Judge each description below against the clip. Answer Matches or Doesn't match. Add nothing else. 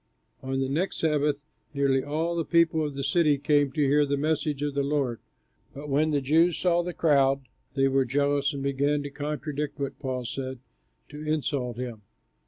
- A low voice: Doesn't match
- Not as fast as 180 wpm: Doesn't match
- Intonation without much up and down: Matches